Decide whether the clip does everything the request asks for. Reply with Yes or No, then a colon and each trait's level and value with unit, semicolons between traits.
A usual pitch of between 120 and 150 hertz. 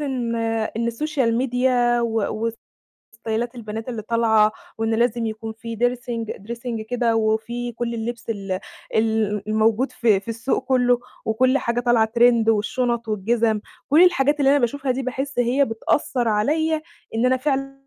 No: high, 235 Hz